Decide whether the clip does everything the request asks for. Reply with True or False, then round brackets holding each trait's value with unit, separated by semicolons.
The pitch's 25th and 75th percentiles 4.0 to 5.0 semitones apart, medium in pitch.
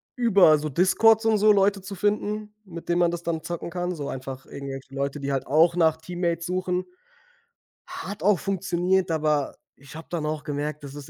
True (4.3 semitones; 170 Hz)